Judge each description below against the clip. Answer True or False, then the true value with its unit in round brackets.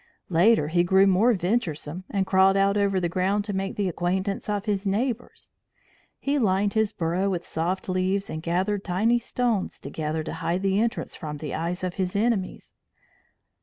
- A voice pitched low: False (190 Hz)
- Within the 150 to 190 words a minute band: True (175 wpm)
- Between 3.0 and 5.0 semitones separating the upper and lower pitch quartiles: False (2.6 semitones)